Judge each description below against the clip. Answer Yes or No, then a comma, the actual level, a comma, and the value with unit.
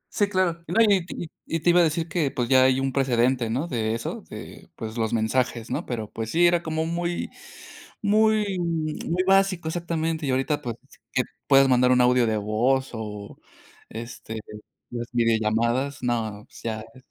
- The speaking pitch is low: Yes, low, 130 Hz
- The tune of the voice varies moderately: No, wide, 6.3 semitones